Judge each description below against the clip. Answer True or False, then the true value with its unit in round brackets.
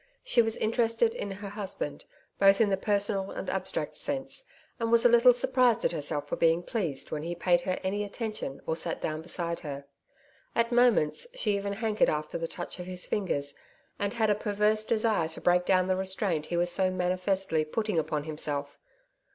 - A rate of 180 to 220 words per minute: True (190 wpm)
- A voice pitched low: False (195 Hz)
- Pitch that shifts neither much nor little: True (4.5 semitones)